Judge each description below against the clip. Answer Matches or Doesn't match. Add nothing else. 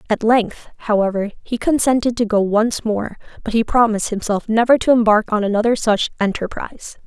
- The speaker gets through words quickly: Doesn't match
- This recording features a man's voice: Doesn't match